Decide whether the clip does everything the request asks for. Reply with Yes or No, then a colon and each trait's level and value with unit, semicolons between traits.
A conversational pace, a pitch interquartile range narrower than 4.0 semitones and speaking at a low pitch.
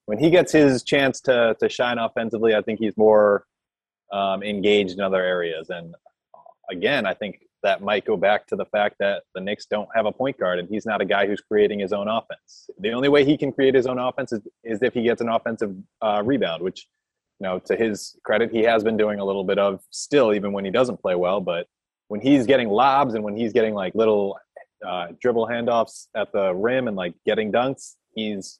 No: fast, 225 wpm; average, 2.9 semitones; low, 105 Hz